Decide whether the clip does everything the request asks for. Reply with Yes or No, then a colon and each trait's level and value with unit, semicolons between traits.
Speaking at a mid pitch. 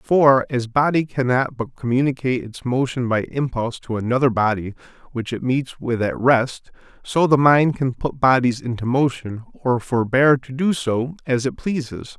No: low, 130 Hz